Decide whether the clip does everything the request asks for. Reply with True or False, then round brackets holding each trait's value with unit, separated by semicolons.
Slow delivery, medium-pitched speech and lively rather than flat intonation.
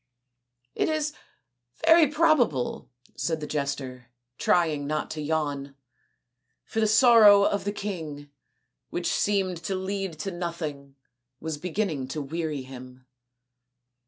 True (125 wpm; 160 Hz; 6.2 semitones)